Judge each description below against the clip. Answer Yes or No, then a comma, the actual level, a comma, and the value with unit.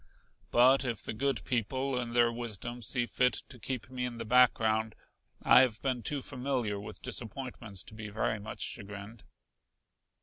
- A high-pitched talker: No, low, 120 Hz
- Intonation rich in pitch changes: No, average, 2.7 semitones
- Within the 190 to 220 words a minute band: No, average, 165 wpm